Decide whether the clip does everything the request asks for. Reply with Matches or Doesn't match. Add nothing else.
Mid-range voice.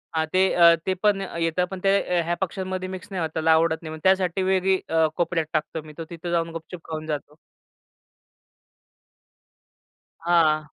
Matches